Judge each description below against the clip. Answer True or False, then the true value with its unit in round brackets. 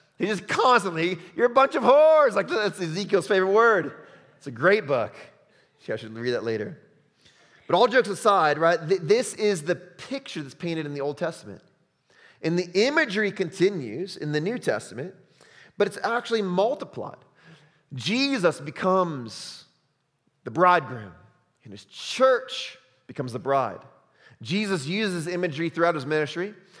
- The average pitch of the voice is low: False (180 Hz)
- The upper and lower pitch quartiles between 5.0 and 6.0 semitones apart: True (5.3 semitones)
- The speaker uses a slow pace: False (150 wpm)